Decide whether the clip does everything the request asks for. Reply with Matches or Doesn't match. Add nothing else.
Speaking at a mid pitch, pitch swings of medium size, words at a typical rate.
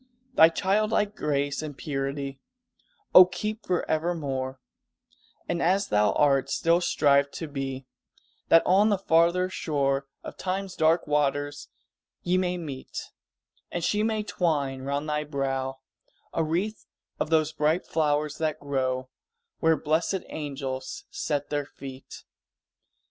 Doesn't match